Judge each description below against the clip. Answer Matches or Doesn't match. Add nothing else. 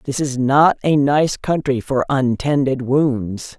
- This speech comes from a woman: Matches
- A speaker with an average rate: Matches